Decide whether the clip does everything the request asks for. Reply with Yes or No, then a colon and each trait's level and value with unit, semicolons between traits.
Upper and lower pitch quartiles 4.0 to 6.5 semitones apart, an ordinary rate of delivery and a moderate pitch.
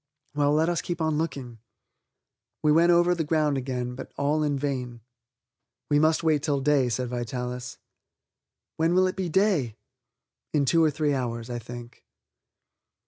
Yes: average, 4.3 semitones; average, 160 wpm; medium, 145 Hz